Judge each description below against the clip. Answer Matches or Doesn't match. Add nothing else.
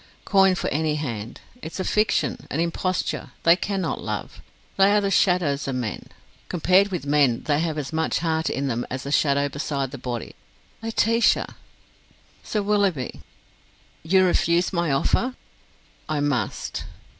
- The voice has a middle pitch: Matches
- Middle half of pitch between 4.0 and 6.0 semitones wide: Matches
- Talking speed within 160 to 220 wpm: Doesn't match